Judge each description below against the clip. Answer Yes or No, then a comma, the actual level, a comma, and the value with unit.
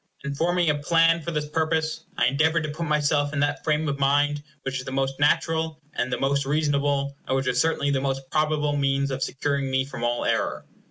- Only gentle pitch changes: Yes, narrow, 2.2 semitones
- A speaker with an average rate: No, fast, 220 wpm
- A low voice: No, medium, 145 Hz